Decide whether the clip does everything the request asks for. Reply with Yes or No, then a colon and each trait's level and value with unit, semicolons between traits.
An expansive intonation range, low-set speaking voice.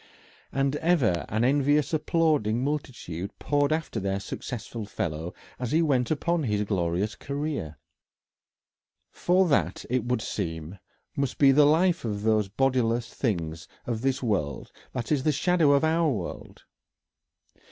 Yes: wide, 6.5 semitones; low, 125 Hz